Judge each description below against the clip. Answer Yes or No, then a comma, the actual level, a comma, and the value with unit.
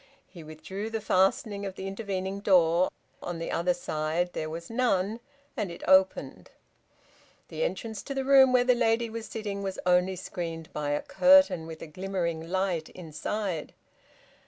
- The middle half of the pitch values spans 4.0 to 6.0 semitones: Yes, average, 4.4 semitones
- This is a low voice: No, high, 190 Hz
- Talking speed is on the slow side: No, average, 160 wpm